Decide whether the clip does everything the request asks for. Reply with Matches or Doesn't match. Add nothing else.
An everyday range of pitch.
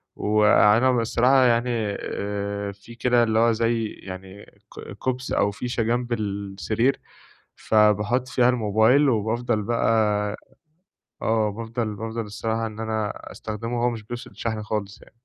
Doesn't match